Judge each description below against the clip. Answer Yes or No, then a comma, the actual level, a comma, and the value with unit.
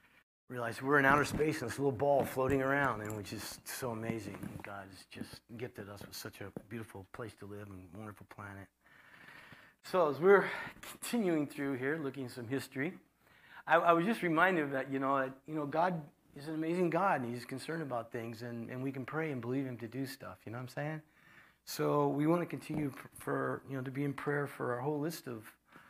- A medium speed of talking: No, fast, 220 wpm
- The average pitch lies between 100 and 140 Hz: Yes, low, 135 Hz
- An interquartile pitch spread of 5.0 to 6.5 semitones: No, average, 4.3 semitones